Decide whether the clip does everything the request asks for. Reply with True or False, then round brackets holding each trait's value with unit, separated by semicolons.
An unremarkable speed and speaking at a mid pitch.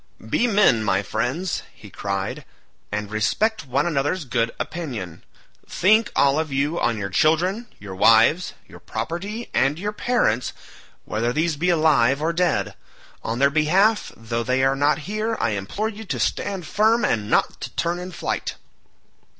True (160 wpm; 150 Hz)